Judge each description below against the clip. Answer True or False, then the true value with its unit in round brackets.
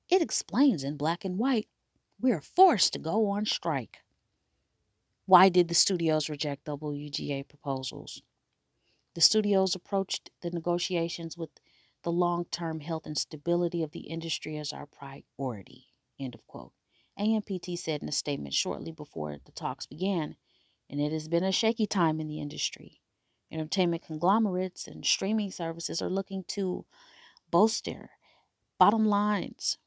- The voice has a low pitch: False (170 Hz)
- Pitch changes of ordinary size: True (4.2 semitones)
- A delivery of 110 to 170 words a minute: True (145 wpm)